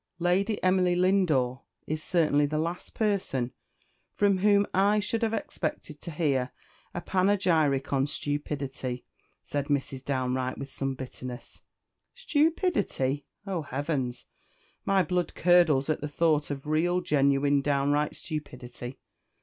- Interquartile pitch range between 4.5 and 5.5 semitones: Yes, average, 5.0 semitones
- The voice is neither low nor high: Yes, medium, 150 Hz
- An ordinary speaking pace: No, slow, 125 wpm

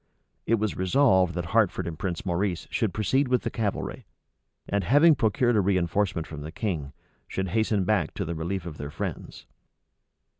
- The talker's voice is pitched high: No, very low, 95 Hz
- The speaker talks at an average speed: Yes, average, 175 wpm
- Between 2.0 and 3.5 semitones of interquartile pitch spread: No, average, 4.2 semitones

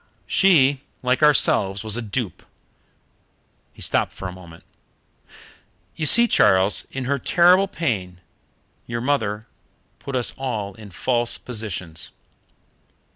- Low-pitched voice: Yes, low, 120 Hz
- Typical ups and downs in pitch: No, wide, 5.9 semitones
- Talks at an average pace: No, slow, 130 wpm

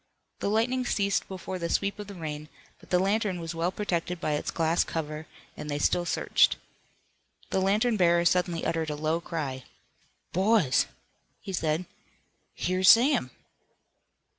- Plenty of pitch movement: No, average, 3.7 semitones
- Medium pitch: Yes, medium, 175 Hz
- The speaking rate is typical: Yes, average, 150 wpm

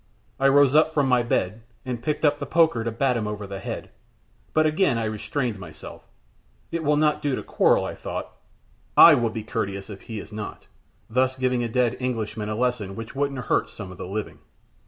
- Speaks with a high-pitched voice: No, low, 120 Hz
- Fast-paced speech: Yes, fast, 210 wpm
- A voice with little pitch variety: No, average, 4.6 semitones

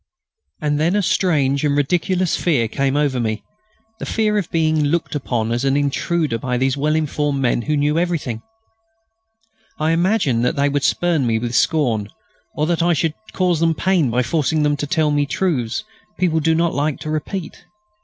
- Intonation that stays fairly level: No, average, 3.7 semitones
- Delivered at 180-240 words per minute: Yes, average, 185 wpm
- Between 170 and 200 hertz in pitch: No, medium, 150 Hz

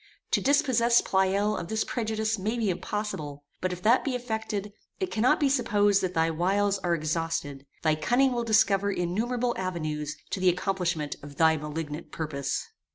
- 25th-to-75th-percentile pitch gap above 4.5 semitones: Yes, average, 5.2 semitones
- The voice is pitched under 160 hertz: No, high, 190 Hz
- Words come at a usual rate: Yes, average, 165 wpm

